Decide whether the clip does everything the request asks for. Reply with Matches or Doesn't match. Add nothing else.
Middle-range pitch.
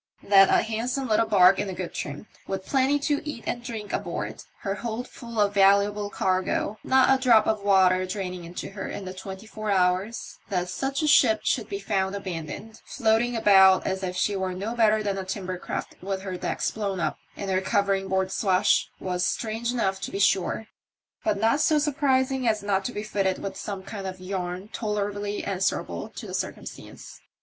Doesn't match